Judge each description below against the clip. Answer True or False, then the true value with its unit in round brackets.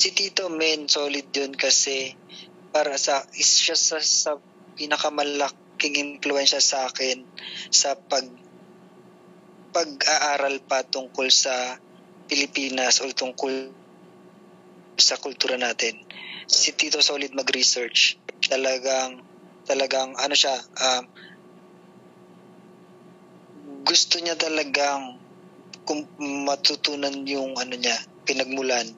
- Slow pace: True (95 wpm)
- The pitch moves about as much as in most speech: False (2.3 semitones)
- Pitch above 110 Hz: True (140 Hz)